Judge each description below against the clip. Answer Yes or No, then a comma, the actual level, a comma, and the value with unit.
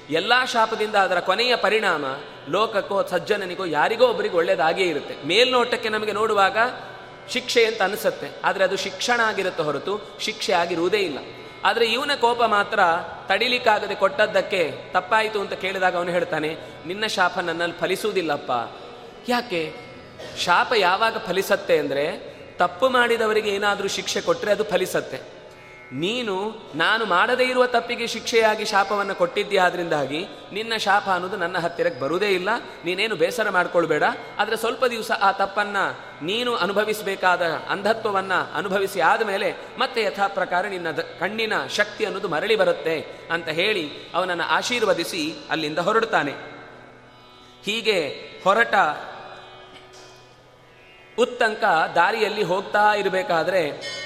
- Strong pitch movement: No, average, 4.3 semitones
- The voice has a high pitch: Yes, high, 205 Hz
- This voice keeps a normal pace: No, fast, 115 wpm